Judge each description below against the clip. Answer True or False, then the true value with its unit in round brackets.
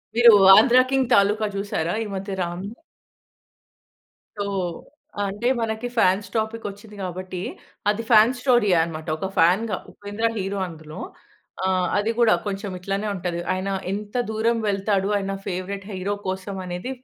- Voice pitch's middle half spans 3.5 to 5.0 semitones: False (2.8 semitones)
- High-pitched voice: True (200 Hz)